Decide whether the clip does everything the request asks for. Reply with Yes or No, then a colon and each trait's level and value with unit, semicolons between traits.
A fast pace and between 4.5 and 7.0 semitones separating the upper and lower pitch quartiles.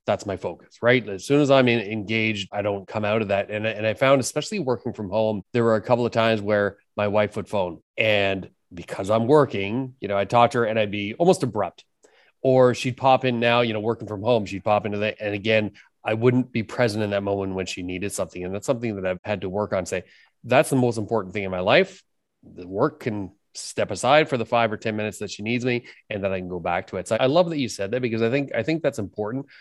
No: fast, 270 wpm; average, 3.2 semitones